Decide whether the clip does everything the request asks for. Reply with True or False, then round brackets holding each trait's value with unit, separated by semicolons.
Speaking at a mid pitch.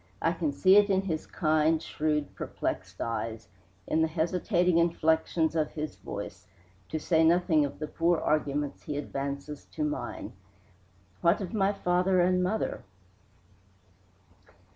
True (160 Hz)